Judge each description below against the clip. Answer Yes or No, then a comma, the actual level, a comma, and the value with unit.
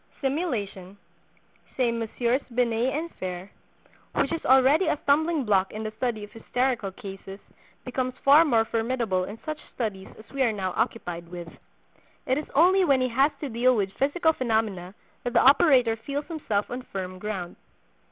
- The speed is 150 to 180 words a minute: Yes, average, 165 wpm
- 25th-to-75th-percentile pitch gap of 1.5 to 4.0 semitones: No, average, 5.1 semitones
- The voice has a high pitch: Yes, high, 235 Hz